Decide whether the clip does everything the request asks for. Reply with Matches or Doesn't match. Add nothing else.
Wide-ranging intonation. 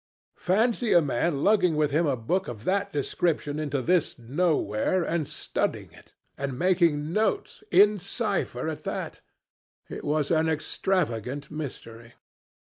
Doesn't match